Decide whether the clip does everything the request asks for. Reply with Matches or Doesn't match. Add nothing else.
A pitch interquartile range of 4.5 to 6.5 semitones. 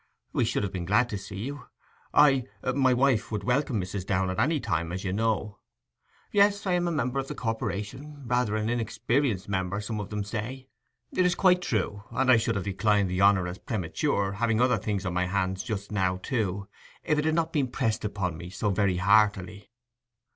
Matches